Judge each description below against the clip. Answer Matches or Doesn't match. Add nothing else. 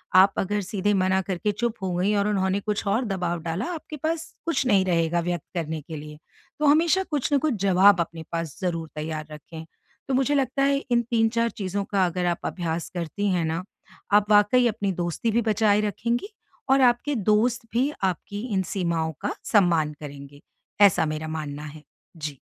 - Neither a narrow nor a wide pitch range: Doesn't match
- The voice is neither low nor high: Doesn't match